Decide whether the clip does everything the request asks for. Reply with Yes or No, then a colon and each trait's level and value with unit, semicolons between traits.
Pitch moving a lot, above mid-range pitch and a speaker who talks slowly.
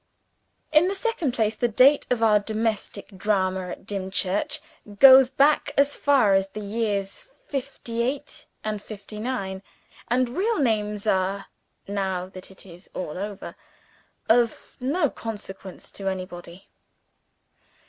No: average, 4.6 semitones; high, 210 Hz; slow, 130 wpm